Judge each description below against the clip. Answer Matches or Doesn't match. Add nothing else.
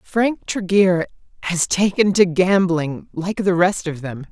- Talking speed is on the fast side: Doesn't match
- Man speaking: Doesn't match